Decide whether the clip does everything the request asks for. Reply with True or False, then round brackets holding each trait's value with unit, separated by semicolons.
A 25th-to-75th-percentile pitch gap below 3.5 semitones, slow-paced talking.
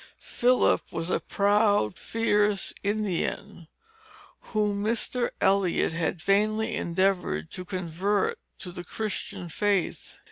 True (3.0 semitones; 105 wpm)